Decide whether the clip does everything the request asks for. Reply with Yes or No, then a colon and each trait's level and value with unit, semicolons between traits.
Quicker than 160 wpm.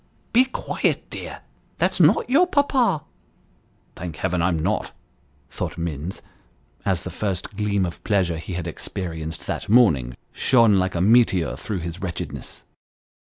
No: average, 155 wpm